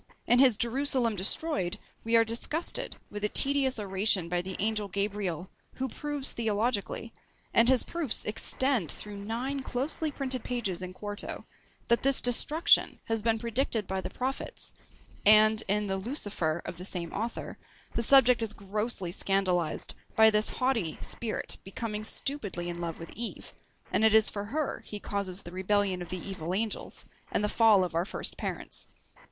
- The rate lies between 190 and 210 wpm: No, average, 165 wpm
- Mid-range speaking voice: No, high, 215 Hz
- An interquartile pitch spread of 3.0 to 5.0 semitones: Yes, average, 4.1 semitones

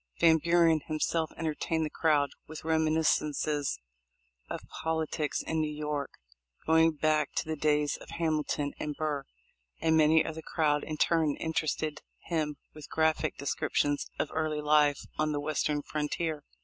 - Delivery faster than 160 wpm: No, average, 150 wpm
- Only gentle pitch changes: Yes, narrow, 1.3 semitones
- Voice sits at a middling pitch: Yes, medium, 155 Hz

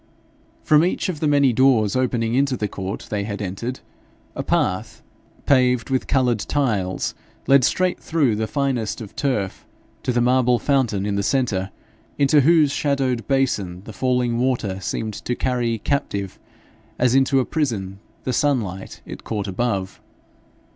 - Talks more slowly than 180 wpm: Yes, average, 155 wpm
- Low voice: Yes, low, 125 Hz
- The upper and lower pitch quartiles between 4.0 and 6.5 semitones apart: Yes, average, 4.5 semitones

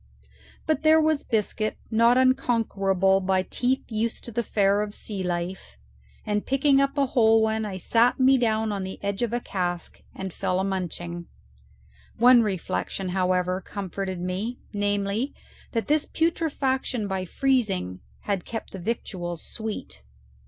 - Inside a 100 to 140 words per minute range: No, average, 150 wpm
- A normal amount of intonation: Yes, average, 4.4 semitones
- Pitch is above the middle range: Yes, high, 210 Hz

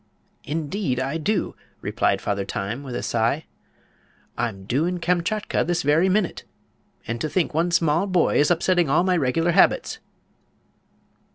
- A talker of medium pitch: Yes, medium, 160 Hz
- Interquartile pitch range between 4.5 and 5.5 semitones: Yes, average, 5.2 semitones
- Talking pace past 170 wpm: No, average, 150 wpm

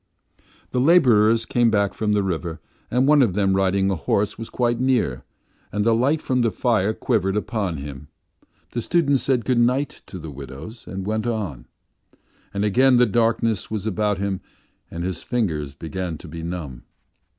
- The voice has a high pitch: No, low, 105 Hz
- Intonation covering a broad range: No, average, 4.8 semitones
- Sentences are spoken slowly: No, average, 175 wpm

